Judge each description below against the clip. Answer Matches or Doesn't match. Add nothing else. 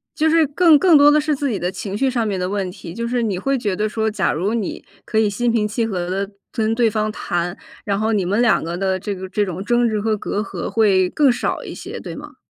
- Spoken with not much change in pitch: Doesn't match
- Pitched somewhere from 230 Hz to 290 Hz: Doesn't match